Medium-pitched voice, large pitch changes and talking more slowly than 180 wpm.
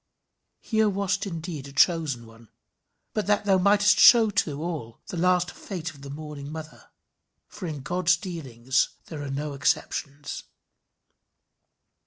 No: medium, 160 Hz; average, 5.0 semitones; average, 140 wpm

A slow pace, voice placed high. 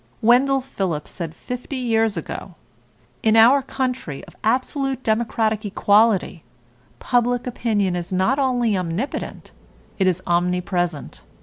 Yes: slow, 115 wpm; high, 220 Hz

